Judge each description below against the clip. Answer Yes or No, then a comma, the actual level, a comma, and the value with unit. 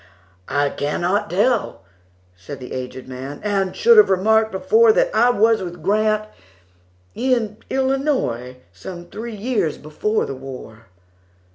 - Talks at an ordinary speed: No, slow, 110 wpm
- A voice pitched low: No, high, 190 Hz